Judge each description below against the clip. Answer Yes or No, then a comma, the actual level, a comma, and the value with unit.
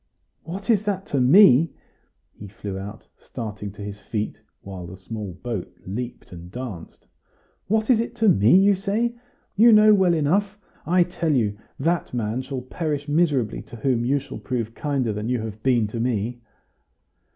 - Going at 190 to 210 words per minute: No, average, 175 wpm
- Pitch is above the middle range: No, low, 125 Hz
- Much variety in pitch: Yes, wide, 8.6 semitones